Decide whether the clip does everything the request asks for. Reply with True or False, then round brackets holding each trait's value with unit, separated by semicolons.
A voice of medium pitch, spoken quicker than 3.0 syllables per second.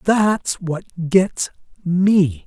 False (180 Hz; 2.0 syllables/s)